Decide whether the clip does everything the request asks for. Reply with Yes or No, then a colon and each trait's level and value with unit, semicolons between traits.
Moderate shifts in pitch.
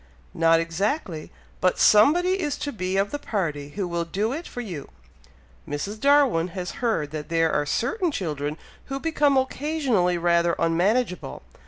No: wide, 8.5 semitones